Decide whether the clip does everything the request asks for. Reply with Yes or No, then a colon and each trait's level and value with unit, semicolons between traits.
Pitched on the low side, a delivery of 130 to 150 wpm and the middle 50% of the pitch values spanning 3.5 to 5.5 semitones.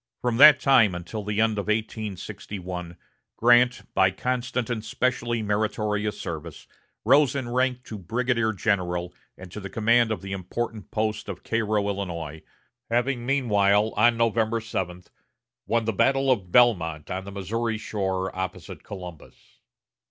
Yes: low, 110 Hz; average, 145 wpm; average, 3.9 semitones